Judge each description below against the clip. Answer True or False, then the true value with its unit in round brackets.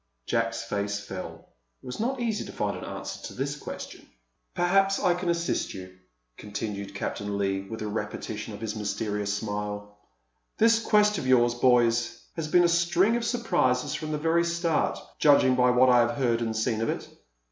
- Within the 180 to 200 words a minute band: True (185 wpm)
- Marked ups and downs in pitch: True (8.4 semitones)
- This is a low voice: True (125 Hz)